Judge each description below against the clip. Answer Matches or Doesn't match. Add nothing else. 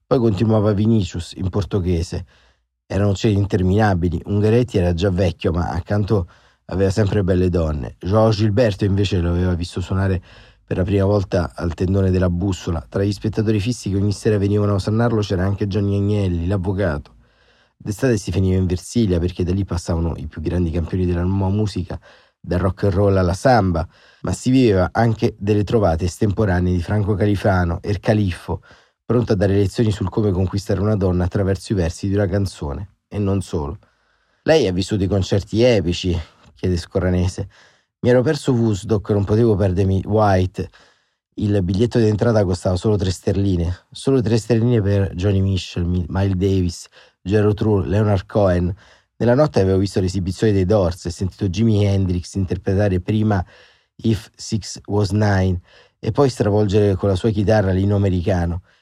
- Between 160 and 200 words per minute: Matches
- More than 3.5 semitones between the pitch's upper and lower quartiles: Doesn't match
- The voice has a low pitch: Matches